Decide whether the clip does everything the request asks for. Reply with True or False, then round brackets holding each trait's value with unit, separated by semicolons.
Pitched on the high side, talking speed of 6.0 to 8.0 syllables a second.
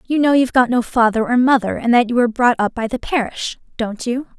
True (240 Hz; 6.1 syllables/s)